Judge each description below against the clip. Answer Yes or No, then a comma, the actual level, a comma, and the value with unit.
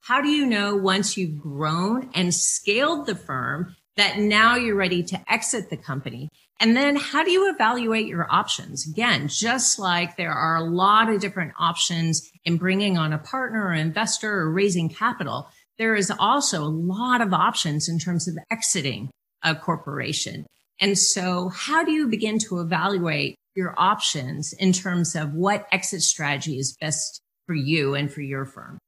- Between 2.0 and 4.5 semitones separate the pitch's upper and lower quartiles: No, average, 5.2 semitones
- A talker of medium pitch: Yes, medium, 180 Hz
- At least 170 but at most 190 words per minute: Yes, average, 175 wpm